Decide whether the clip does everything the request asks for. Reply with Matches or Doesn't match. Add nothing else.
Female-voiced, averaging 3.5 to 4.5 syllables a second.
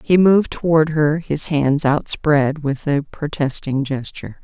Matches